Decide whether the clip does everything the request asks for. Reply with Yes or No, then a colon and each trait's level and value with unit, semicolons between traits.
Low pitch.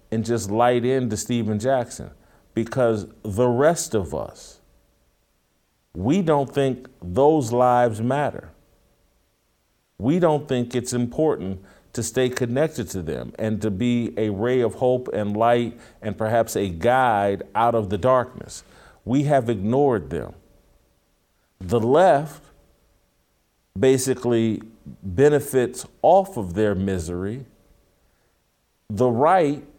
Yes: low, 115 Hz